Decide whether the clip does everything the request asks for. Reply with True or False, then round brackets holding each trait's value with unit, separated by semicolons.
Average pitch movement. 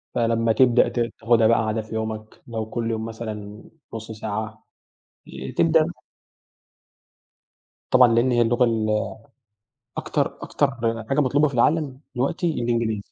False (2.1 semitones)